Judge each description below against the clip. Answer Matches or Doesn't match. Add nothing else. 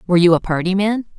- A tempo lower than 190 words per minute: Doesn't match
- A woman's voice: Matches